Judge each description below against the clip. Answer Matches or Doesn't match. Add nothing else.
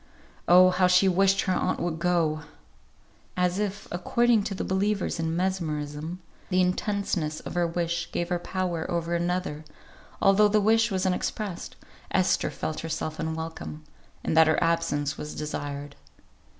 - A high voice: Doesn't match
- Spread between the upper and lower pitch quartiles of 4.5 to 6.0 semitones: Doesn't match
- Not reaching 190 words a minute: Matches